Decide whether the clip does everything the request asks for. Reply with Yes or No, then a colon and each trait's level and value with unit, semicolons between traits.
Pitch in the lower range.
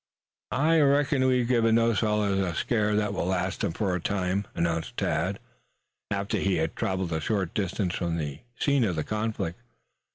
Yes: low, 100 Hz